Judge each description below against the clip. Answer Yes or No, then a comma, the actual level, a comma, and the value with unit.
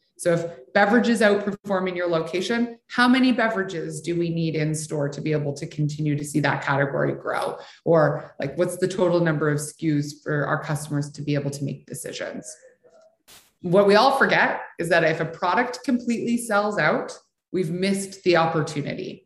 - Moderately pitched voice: Yes, medium, 170 Hz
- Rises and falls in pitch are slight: No, average, 5.0 semitones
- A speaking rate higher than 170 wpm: Yes, average, 180 wpm